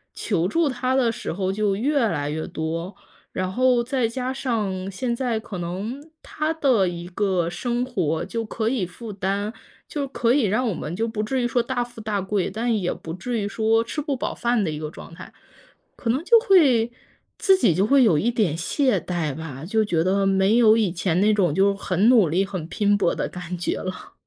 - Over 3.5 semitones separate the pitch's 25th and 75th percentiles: Yes, average, 5.0 semitones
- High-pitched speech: Yes, high, 210 Hz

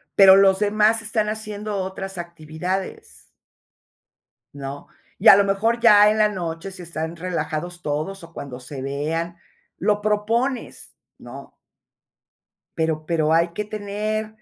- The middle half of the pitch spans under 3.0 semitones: No, average, 4.3 semitones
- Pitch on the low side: No, high, 190 Hz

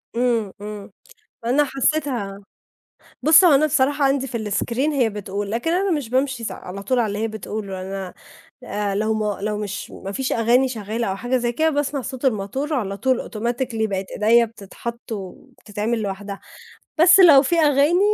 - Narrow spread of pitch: No, average, 4.8 semitones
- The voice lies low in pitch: No, high, 235 Hz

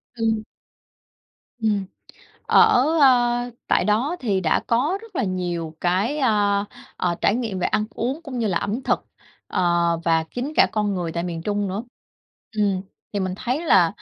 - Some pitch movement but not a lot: Yes, average, 4.8 semitones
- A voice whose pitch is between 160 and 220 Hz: Yes, high, 210 Hz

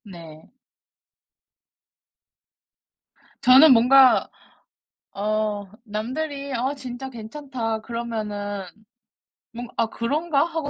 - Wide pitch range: No, average, 4.2 semitones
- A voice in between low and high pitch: No, high, 240 Hz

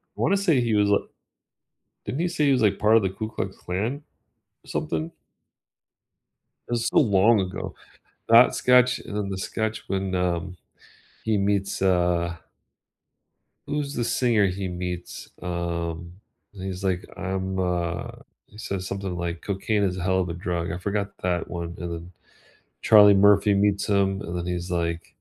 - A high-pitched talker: No, very low, 95 Hz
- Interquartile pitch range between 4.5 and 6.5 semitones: No, average, 2.9 semitones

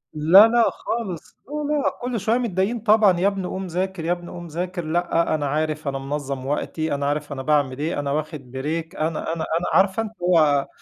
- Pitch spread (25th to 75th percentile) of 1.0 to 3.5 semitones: No, average, 4.2 semitones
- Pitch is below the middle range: No, medium, 165 Hz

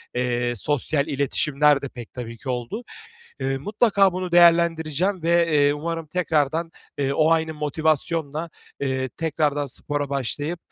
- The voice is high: No, medium, 150 Hz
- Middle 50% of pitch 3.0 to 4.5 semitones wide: Yes, average, 3.3 semitones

